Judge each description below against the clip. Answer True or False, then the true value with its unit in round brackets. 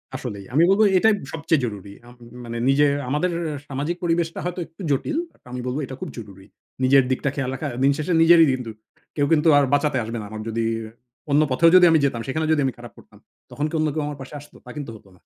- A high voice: False (140 Hz)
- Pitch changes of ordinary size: True (4.4 semitones)